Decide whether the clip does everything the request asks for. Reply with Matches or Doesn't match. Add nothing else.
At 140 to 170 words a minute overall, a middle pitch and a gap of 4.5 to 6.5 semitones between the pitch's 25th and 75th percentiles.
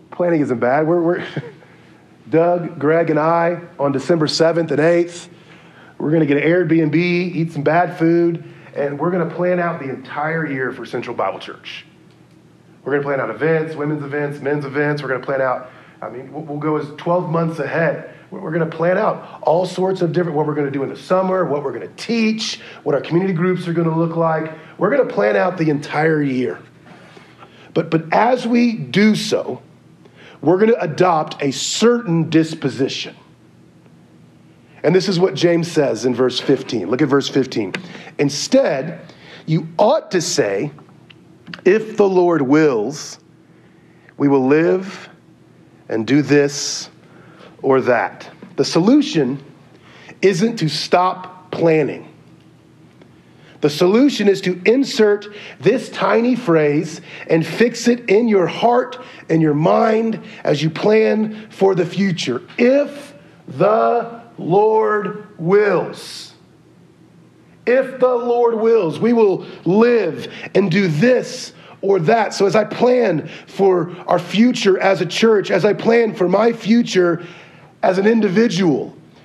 Matches